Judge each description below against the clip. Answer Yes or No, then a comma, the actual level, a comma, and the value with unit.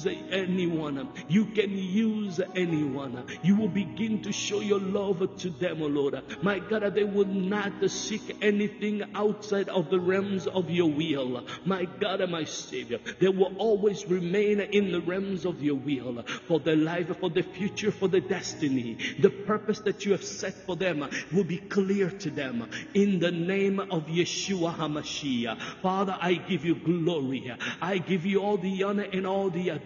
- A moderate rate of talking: Yes, average, 175 wpm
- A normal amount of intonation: Yes, average, 3.0 semitones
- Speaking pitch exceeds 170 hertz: Yes, high, 190 Hz